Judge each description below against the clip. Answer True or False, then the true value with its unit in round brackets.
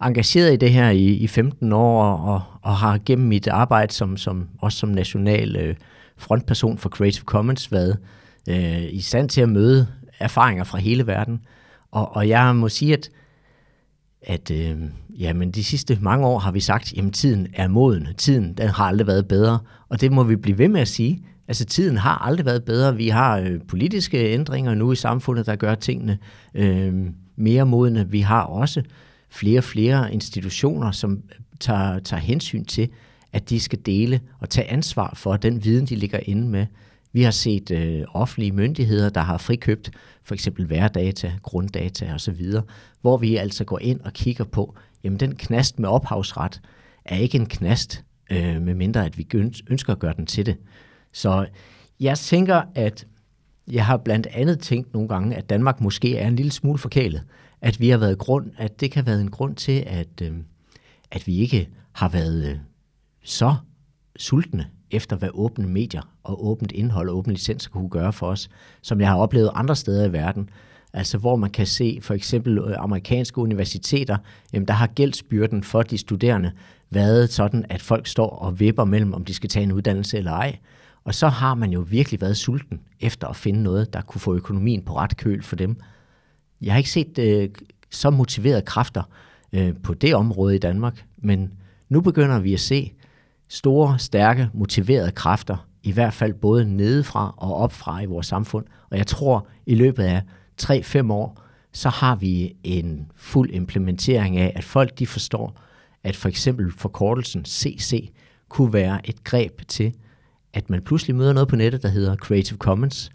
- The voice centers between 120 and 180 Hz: False (110 Hz)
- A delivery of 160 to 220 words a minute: True (180 wpm)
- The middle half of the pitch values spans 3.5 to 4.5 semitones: True (4.2 semitones)